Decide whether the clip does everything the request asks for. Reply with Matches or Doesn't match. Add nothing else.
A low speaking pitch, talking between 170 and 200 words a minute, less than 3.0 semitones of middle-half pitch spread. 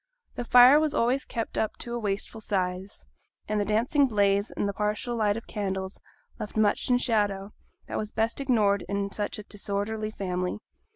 Doesn't match